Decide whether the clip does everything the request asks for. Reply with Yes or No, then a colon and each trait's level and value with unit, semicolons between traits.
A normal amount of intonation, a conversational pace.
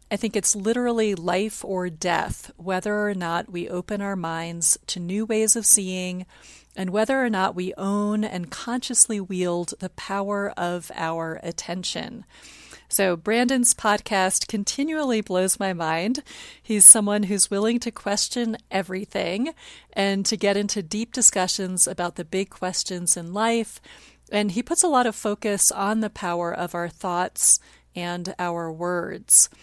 Yes: average, 3.3 semitones; average, 150 wpm